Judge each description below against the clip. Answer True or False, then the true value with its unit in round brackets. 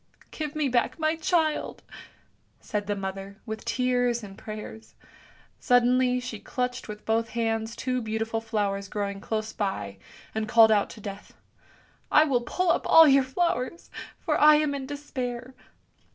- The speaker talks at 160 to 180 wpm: True (165 wpm)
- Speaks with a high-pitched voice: True (240 Hz)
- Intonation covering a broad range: False (3.7 semitones)